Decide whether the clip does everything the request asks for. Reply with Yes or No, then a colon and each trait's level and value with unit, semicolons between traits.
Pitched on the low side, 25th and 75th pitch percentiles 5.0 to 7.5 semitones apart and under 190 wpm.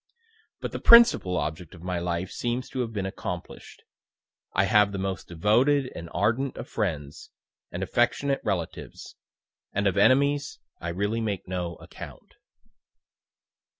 Yes: low, 100 Hz; average, 5.3 semitones; average, 140 wpm